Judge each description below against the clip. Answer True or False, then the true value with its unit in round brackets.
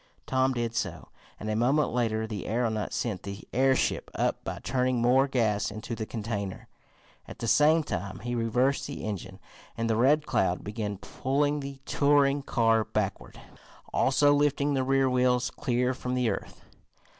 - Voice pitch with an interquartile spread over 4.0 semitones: False (3.4 semitones)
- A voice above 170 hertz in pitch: False (125 Hz)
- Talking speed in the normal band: True (165 wpm)